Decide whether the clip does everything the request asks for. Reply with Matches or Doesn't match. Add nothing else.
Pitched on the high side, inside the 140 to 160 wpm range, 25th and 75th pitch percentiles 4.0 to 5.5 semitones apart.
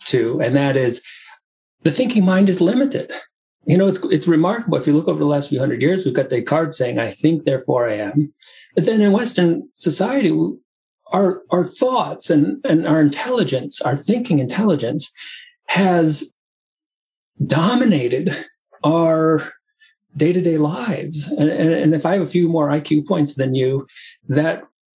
Doesn't match